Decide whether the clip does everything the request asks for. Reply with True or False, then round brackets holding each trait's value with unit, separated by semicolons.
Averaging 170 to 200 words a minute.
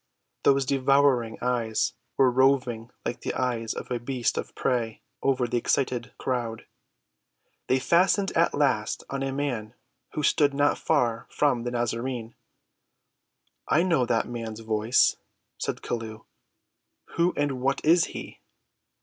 False (135 wpm)